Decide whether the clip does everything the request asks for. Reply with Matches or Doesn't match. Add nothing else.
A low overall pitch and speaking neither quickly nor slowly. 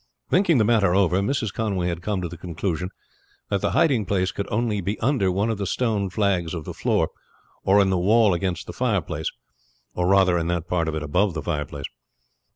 Doesn't match